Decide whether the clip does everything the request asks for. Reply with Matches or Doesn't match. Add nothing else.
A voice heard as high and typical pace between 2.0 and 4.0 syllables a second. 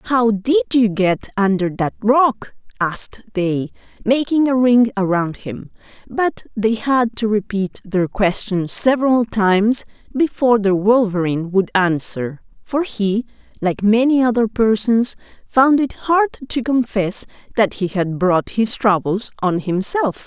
Matches